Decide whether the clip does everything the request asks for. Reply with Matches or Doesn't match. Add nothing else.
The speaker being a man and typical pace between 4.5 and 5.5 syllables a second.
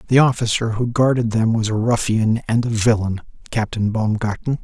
Matches